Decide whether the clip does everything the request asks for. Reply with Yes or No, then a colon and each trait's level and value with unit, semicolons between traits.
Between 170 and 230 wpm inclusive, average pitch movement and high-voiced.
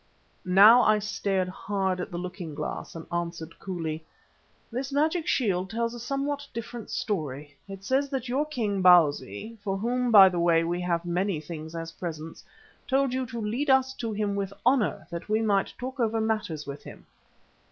No: average, 180 wpm; wide, 5.9 semitones; high, 200 Hz